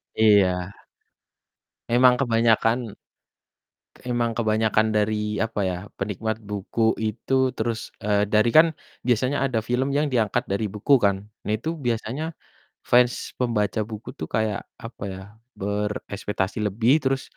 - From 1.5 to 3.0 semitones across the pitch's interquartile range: Yes, narrow, 2.6 semitones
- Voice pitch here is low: Yes, low, 110 Hz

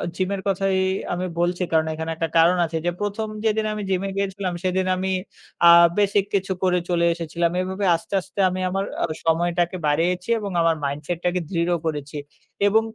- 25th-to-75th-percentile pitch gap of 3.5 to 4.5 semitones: No, narrow, 2.5 semitones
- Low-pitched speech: No, medium, 180 Hz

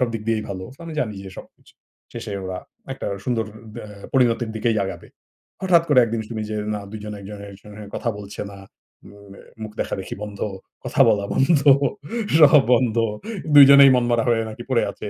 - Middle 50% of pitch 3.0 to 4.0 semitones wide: Yes, average, 3.4 semitones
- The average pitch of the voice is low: Yes, low, 115 Hz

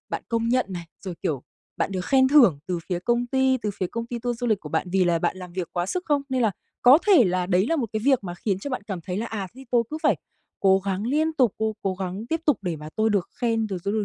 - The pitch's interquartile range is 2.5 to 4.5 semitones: No, average, 5.1 semitones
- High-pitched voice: Yes, high, 215 Hz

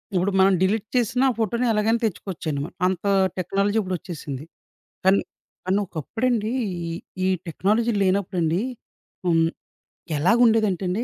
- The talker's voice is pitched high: Yes, high, 195 Hz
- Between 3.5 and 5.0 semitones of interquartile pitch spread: Yes, average, 3.9 semitones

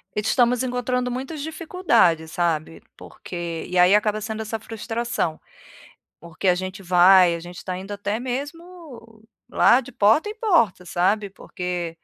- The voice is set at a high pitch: Yes, high, 210 Hz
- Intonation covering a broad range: Yes, wide, 5.7 semitones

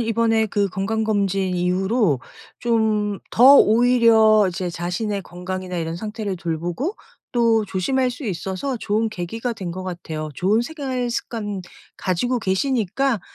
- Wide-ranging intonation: No, average, 4.0 semitones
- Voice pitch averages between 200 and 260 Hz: Yes, high, 210 Hz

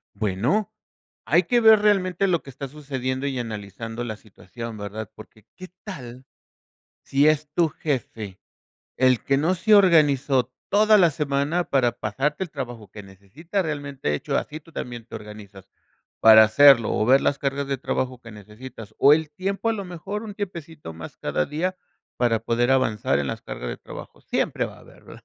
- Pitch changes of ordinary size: No, wide, 6.6 semitones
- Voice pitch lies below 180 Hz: Yes, low, 135 Hz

